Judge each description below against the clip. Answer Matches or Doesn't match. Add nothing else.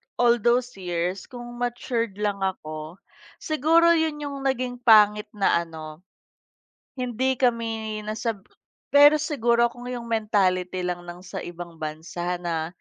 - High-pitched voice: Matches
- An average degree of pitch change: Doesn't match